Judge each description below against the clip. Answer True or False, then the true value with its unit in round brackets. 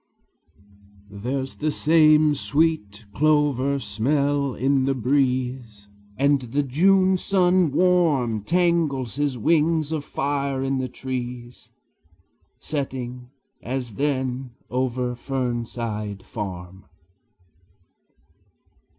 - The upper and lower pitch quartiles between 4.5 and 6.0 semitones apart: False (3.3 semitones)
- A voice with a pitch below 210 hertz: True (135 Hz)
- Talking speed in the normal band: False (90 wpm)